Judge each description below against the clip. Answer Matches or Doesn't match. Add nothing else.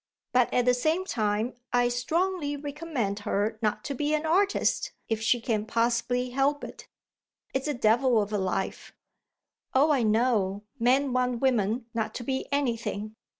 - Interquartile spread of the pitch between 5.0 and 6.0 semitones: Doesn't match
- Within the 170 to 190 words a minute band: Doesn't match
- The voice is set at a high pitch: Matches